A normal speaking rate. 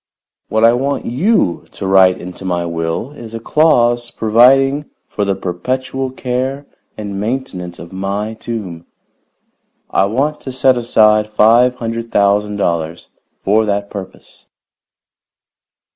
No: slow, 130 wpm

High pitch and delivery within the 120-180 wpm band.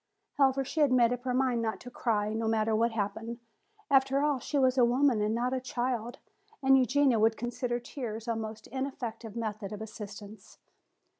No: high, 235 Hz; average, 190 wpm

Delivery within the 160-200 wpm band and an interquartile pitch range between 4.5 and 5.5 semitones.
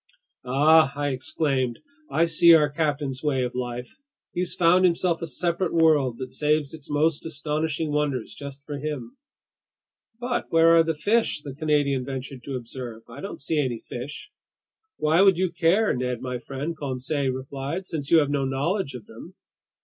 No: average, 170 wpm; average, 3.7 semitones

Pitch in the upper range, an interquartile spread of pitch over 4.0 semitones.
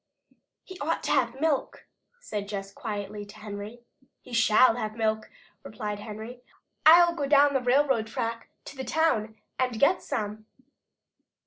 Yes: high, 230 Hz; average, 4.7 semitones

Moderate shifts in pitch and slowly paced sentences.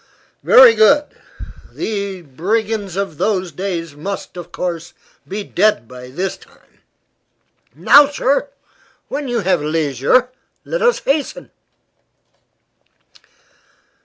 No: wide, 6.0 semitones; slow, 105 wpm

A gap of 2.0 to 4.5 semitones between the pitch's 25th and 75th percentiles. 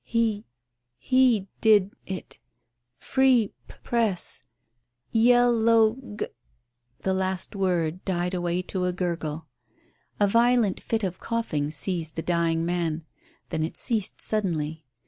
No: average, 5.0 semitones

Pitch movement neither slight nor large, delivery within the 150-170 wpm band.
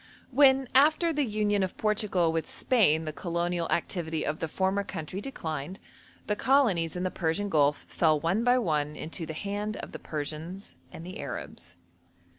Yes: average, 4.8 semitones; average, 165 wpm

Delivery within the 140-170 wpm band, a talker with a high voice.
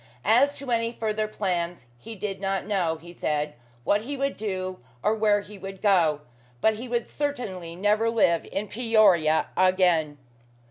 Yes: average, 160 wpm; high, 200 Hz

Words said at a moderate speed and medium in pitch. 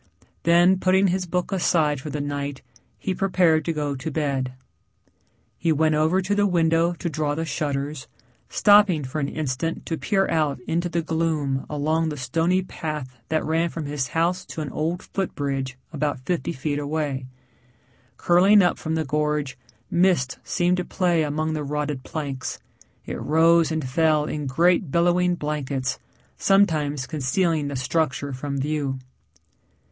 Yes: average, 160 wpm; medium, 155 Hz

